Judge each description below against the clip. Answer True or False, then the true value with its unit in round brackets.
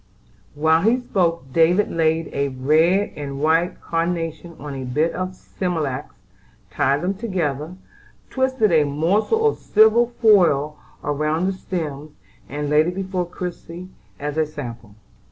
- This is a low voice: False (165 Hz)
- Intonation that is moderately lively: True (4.0 semitones)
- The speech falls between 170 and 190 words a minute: False (135 wpm)